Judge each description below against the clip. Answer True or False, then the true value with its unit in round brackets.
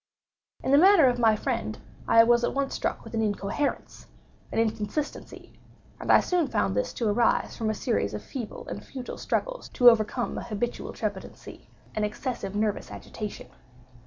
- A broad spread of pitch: False (3.6 semitones)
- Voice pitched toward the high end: True (230 Hz)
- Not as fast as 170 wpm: True (160 wpm)